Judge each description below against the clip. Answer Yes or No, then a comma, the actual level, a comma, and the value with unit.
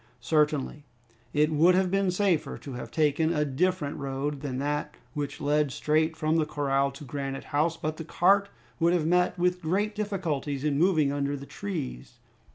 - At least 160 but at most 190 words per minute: Yes, average, 175 wpm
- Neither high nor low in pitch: Yes, medium, 150 Hz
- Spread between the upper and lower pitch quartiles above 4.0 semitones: No, average, 3.7 semitones